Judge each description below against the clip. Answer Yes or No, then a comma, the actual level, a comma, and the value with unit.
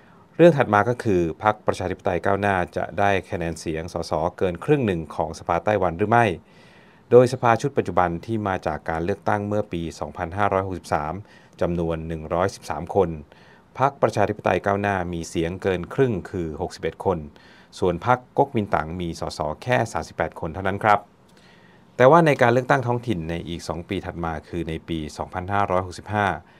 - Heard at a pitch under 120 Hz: Yes, very low, 95 Hz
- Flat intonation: No, average, 3.8 semitones